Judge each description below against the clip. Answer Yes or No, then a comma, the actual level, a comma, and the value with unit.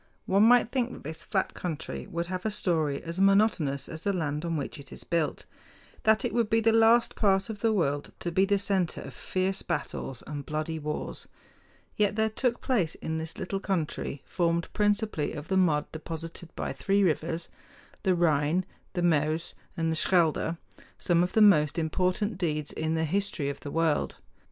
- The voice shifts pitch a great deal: No, average, 4.2 semitones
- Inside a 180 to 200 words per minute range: Yes, average, 190 wpm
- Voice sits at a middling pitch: Yes, medium, 175 Hz